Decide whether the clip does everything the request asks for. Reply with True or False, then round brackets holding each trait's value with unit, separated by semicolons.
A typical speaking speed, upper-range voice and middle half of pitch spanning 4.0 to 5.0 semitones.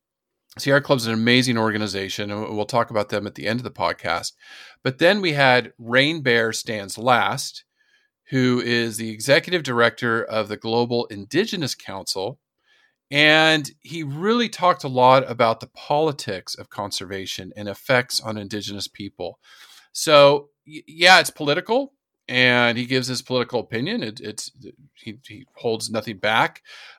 False (155 wpm; 125 Hz; 4.7 semitones)